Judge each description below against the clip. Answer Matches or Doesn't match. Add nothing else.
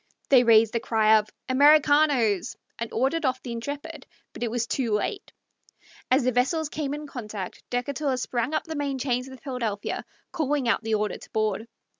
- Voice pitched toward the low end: Doesn't match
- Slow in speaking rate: Doesn't match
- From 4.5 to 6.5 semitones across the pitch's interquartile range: Doesn't match